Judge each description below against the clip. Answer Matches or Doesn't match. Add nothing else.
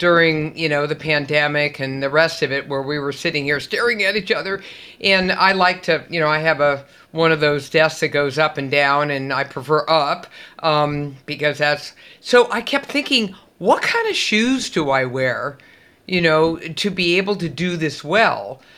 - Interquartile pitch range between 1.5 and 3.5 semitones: Doesn't match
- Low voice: Doesn't match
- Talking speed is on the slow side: Doesn't match